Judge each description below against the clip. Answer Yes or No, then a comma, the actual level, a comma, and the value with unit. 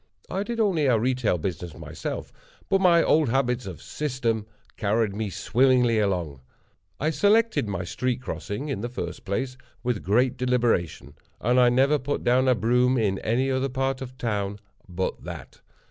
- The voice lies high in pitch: No, low, 125 Hz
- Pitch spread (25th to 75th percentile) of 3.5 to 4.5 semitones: Yes, average, 4.2 semitones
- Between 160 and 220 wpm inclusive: Yes, average, 165 wpm